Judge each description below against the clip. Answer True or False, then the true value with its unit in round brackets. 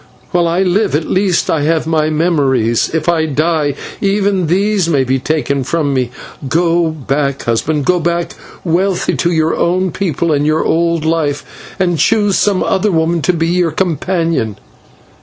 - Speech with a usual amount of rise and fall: True (3.0 semitones)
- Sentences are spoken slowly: False (165 wpm)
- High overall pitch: False (165 Hz)